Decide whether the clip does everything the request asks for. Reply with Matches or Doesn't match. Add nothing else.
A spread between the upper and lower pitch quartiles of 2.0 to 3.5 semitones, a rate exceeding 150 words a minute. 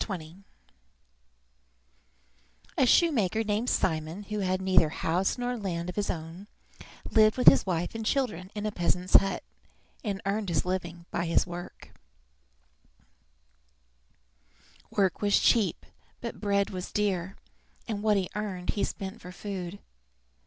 Doesn't match